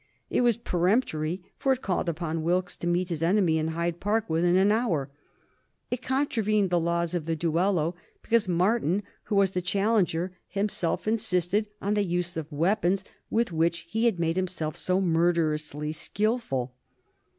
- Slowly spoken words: No, average, 165 wpm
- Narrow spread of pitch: No, average, 3.9 semitones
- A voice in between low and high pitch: Yes, medium, 180 Hz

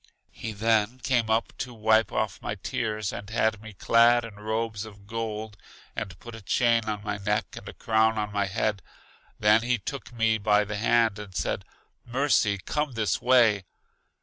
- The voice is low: Yes, low, 110 Hz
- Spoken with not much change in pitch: Yes, narrow, 1.8 semitones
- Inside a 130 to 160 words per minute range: No, average, 180 wpm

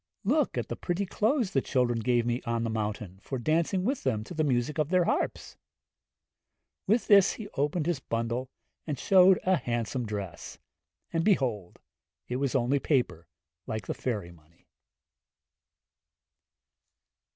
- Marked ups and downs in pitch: Yes, wide, 7.5 semitones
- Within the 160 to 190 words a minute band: No, average, 150 wpm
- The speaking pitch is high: No, low, 130 Hz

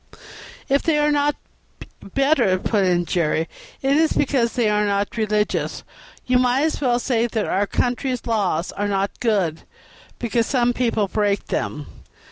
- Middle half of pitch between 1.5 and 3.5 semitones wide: No, average, 4.2 semitones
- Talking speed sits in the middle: Yes, average, 155 wpm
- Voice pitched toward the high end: Yes, high, 230 Hz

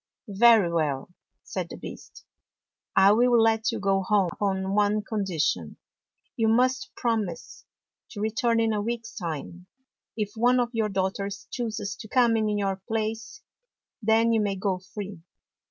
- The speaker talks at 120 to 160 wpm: Yes, average, 155 wpm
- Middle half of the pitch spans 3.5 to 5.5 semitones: No, average, 2.8 semitones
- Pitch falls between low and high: No, high, 210 Hz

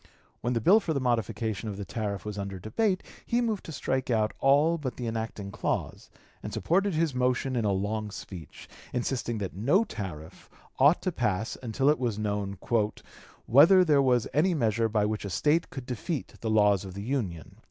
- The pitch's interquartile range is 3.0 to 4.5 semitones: No, wide, 5.6 semitones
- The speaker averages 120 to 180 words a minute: No, average, 195 wpm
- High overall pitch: No, low, 115 Hz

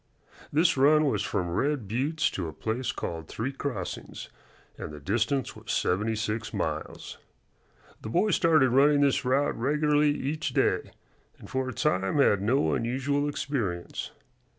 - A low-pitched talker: Yes, low, 130 Hz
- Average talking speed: Yes, average, 150 wpm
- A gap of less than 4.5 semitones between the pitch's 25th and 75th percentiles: No, wide, 5.4 semitones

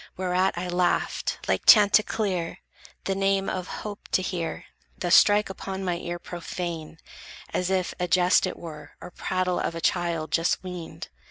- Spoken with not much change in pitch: Yes, narrow, 1.8 semitones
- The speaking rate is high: No, average, 160 wpm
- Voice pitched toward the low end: No, medium, 180 Hz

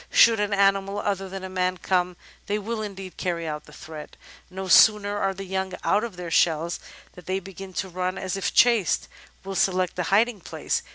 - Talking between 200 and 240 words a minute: Yes, fast, 205 wpm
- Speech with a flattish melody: Yes, narrow, 1.8 semitones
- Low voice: No, high, 190 Hz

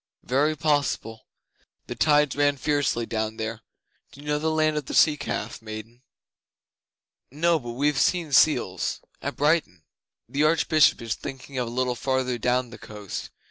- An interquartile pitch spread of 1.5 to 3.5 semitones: No, average, 4.2 semitones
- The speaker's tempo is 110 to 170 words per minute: Yes, average, 160 wpm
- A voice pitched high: No, low, 135 Hz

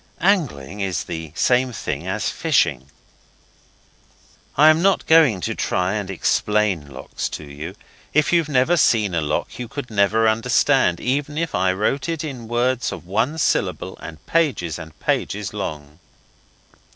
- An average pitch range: No, wide, 8.2 semitones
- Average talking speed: Yes, average, 150 wpm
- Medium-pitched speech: No, low, 110 Hz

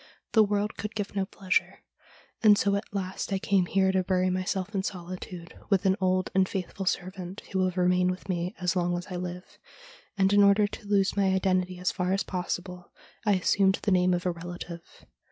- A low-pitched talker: No, medium, 185 Hz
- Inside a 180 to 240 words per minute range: Yes, fast, 205 wpm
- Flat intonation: Yes, narrow, 1.5 semitones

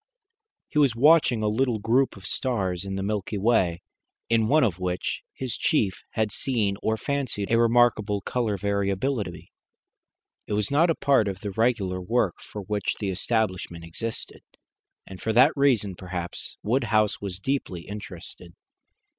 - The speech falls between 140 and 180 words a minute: Yes, average, 155 wpm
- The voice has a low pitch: Yes, low, 105 Hz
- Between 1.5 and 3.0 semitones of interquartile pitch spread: No, average, 4.0 semitones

